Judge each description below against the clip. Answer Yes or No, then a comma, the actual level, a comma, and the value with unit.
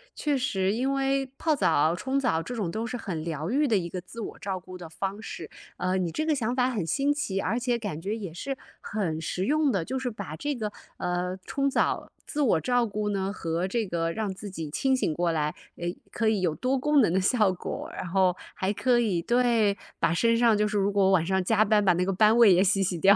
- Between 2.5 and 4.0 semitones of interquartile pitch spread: No, average, 5.0 semitones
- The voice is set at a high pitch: Yes, high, 205 Hz